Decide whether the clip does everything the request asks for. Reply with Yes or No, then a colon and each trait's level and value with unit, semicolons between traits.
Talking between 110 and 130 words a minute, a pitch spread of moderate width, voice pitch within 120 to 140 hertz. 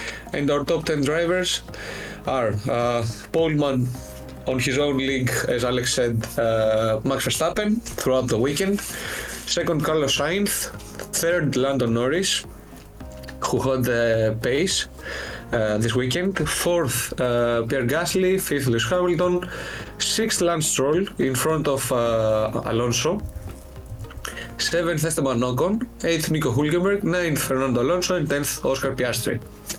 No: average, 125 wpm; wide, 6.0 semitones; low, 135 Hz